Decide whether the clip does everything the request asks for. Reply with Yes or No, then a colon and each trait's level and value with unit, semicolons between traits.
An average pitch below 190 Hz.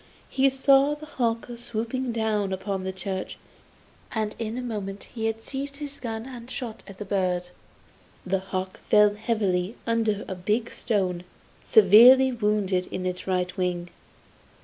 No: high, 215 Hz